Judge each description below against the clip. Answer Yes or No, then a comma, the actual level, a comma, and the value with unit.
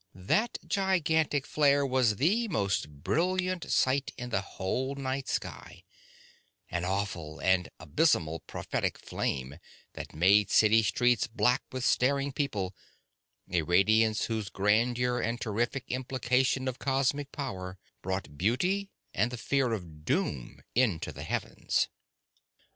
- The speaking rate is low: Yes, slow, 125 wpm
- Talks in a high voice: No, low, 120 Hz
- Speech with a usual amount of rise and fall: No, wide, 6.3 semitones